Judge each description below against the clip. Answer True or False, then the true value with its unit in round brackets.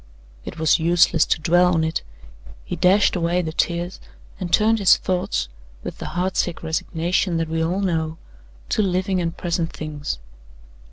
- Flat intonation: True (2.1 semitones)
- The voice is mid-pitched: True (170 Hz)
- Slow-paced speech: False (165 wpm)